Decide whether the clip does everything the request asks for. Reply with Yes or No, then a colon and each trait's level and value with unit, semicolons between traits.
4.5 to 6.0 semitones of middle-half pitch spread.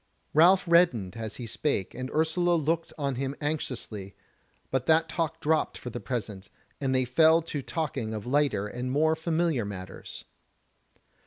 Yes: average, 5.1 semitones